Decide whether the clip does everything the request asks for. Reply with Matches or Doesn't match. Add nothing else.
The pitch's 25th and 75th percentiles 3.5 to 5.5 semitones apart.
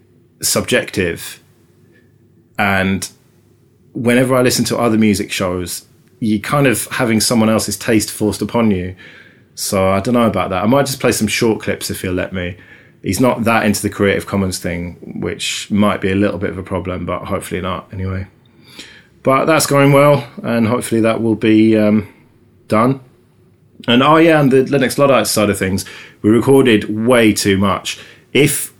Matches